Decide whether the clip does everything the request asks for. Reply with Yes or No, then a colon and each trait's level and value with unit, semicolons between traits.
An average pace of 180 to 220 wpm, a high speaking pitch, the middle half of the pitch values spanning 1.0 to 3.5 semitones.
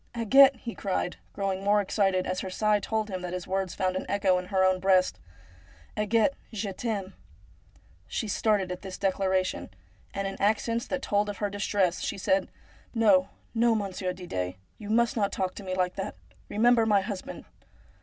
Yes: average, 195 wpm; high, 195 Hz; narrow, 2.4 semitones